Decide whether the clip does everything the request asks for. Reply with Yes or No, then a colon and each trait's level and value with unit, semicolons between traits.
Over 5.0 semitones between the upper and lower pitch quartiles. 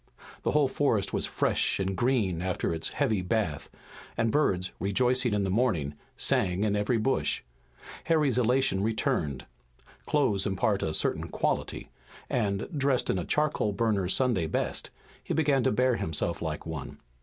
Yes: wide, 5.5 semitones